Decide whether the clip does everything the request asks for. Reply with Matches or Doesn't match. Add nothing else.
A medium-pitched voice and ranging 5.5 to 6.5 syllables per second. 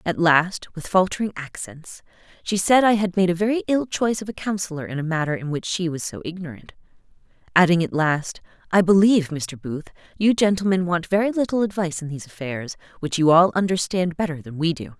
Matches